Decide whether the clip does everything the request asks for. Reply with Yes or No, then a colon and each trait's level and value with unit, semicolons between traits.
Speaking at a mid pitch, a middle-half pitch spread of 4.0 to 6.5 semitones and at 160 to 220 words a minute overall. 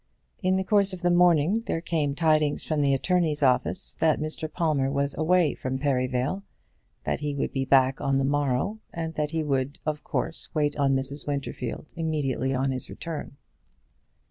No: medium, 145 Hz; average, 3.2 semitones; average, 175 wpm